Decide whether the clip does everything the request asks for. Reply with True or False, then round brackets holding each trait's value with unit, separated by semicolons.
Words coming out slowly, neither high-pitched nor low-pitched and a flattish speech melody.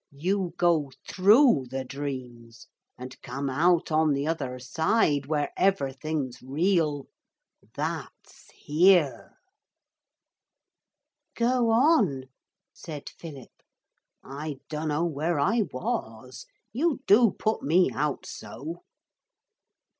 False (95 wpm; 155 Hz; 5.3 semitones)